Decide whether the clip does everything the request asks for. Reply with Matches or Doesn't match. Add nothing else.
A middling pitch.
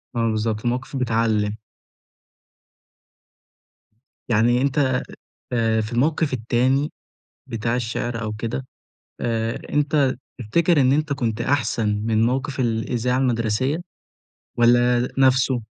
Doesn't match